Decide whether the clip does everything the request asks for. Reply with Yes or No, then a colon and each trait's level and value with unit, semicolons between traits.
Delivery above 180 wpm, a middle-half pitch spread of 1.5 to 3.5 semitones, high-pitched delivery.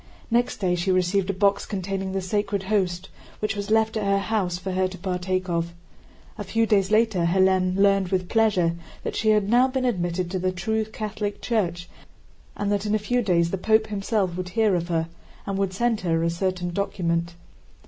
Yes: average, 200 wpm; average, 2.8 semitones; high, 195 Hz